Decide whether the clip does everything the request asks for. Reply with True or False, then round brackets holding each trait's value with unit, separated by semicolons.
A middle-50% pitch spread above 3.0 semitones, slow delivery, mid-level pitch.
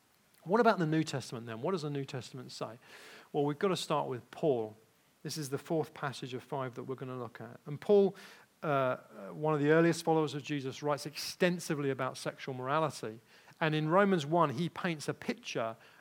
False (3.7 semitones; 205 wpm; 150 Hz)